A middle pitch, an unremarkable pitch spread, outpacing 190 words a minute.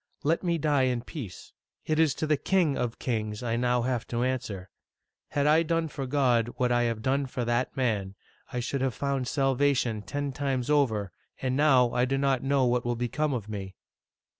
No: low, 130 Hz; average, 3.1 semitones; average, 200 wpm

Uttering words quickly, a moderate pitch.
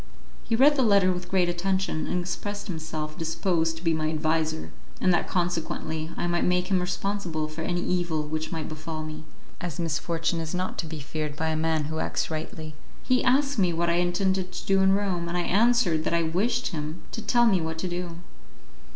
Yes: fast, 210 wpm; medium, 175 Hz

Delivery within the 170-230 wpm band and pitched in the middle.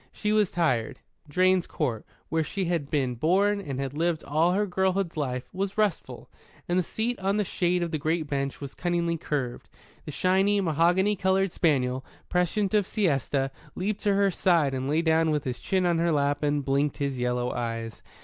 Yes: average, 190 wpm; medium, 165 Hz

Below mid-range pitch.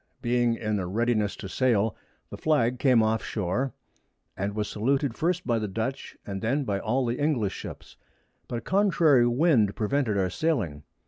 Yes: low, 115 Hz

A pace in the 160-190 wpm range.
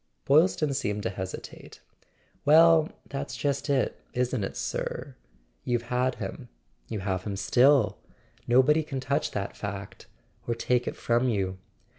No: average, 145 wpm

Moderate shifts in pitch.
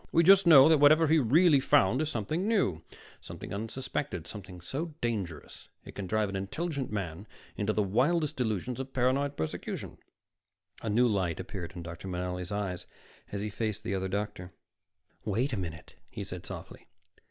No: wide, 6.9 semitones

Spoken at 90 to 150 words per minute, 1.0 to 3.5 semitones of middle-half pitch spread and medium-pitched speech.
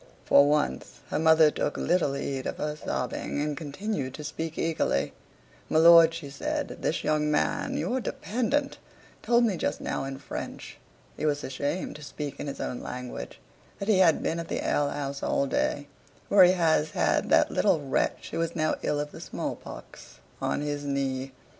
No: average, 185 wpm; average, 3.0 semitones; medium, 150 Hz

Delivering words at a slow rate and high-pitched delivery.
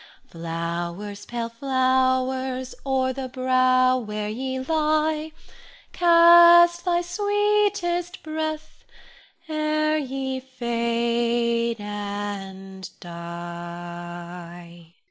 Yes: slow, 70 wpm; very high, 255 Hz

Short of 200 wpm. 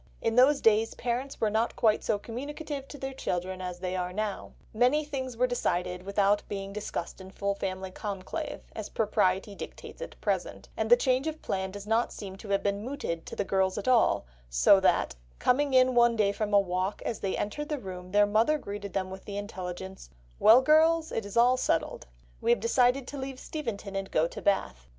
No: fast, 205 wpm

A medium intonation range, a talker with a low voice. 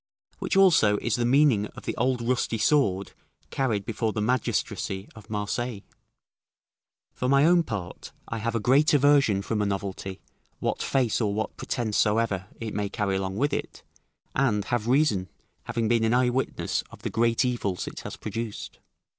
Yes: average, 3.5 semitones; low, 115 Hz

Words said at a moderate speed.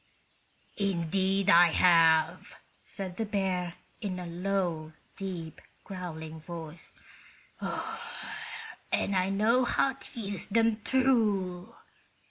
No: slow, 95 wpm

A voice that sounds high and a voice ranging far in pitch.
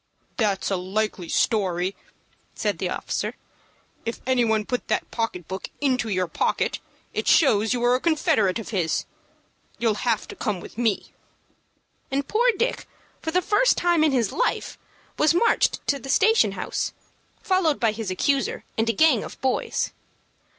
Yes: high, 240 Hz; wide, 6.7 semitones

